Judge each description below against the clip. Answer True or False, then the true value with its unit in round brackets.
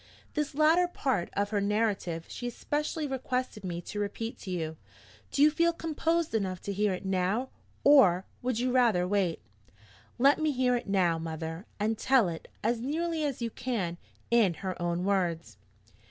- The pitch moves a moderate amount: False (6.6 semitones)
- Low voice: False (215 Hz)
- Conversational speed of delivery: True (170 wpm)